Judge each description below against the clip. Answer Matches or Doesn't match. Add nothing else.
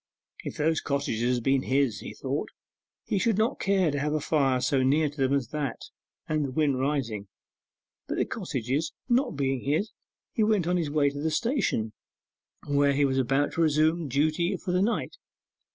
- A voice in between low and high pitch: Matches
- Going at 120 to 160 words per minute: Doesn't match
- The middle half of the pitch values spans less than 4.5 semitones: Matches